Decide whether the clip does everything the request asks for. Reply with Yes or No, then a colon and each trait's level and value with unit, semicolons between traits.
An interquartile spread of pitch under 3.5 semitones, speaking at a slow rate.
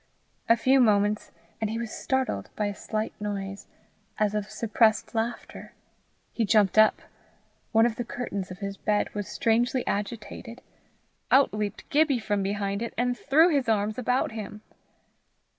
No: average, 2.7 semitones; average, 155 wpm